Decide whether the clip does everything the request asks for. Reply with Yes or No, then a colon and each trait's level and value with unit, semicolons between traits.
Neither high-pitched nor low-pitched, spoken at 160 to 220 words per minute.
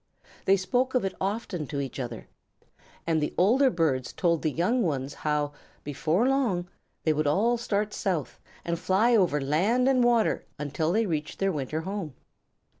Yes: medium, 175 Hz; average, 170 wpm